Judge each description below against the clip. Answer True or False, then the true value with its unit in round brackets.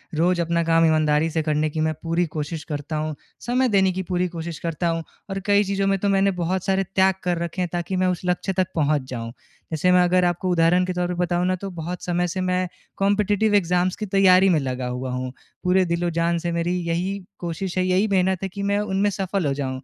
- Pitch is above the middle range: False (180 Hz)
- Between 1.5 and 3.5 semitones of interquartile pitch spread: True (2.5 semitones)